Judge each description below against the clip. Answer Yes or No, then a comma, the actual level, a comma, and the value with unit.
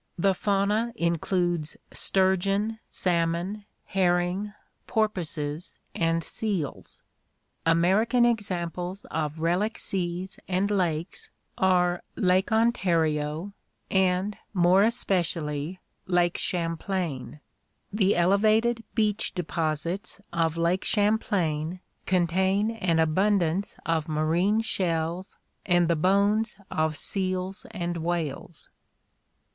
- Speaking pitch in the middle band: Yes, medium, 180 Hz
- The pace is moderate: No, slow, 90 wpm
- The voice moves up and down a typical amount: Yes, average, 3.1 semitones